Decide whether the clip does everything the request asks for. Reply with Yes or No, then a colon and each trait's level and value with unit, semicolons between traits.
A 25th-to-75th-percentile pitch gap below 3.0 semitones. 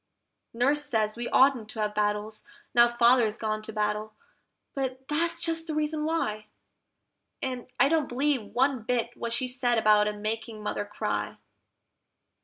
No: average, 4.1 semitones